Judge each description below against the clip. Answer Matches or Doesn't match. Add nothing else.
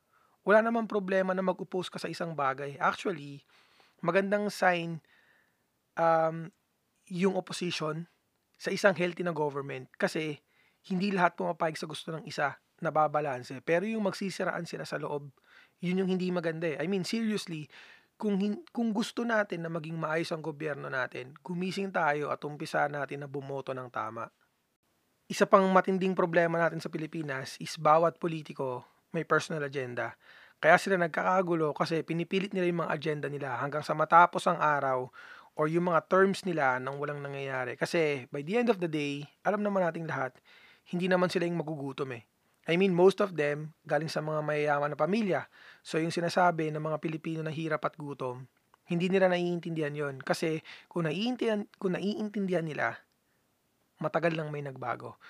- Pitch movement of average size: Matches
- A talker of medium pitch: Matches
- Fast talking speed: Matches